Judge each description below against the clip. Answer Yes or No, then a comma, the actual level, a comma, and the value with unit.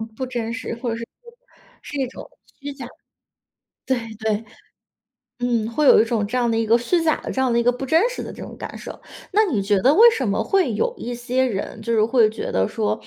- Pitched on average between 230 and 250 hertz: Yes, high, 240 Hz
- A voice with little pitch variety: No, average, 3.2 semitones